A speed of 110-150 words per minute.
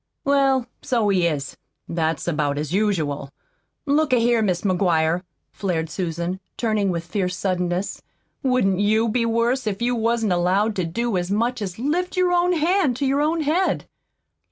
No: average, 165 wpm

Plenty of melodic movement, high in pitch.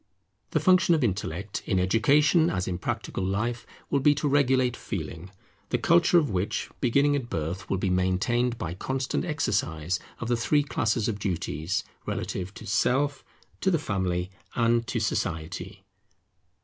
No: wide, 6.9 semitones; low, 115 Hz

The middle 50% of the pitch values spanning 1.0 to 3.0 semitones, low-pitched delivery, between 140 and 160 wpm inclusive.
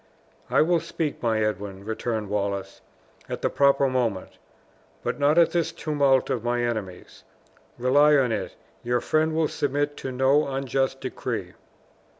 No: average, 4.5 semitones; low, 130 Hz; average, 150 wpm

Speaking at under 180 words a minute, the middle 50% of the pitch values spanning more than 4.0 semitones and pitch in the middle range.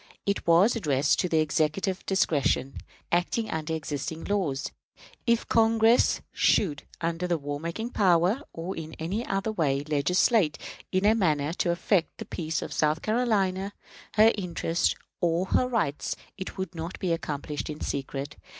Yes: average, 150 wpm; average, 4.5 semitones; medium, 170 Hz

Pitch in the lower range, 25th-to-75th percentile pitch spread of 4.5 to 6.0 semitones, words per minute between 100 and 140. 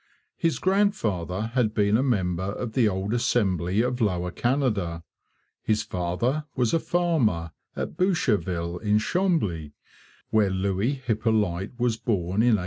Yes: low, 110 Hz; average, 5.3 semitones; slow, 135 wpm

